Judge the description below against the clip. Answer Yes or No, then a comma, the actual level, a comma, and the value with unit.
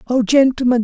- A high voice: Yes, high, 245 Hz